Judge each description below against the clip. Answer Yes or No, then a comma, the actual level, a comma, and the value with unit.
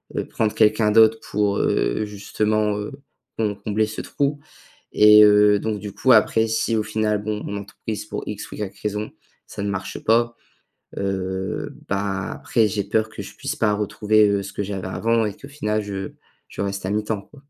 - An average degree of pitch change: No, narrow, 1.3 semitones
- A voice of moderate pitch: No, low, 105 Hz